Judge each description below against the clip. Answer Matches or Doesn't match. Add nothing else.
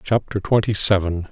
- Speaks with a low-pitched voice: Matches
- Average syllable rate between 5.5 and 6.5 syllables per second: Doesn't match